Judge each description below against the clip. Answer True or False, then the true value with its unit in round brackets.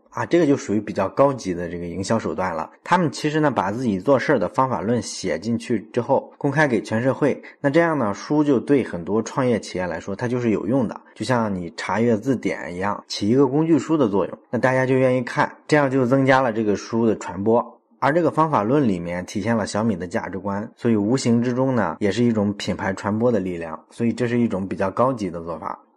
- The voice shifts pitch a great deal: False (4.7 semitones)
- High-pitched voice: False (115 Hz)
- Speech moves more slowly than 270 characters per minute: False (345 characters per minute)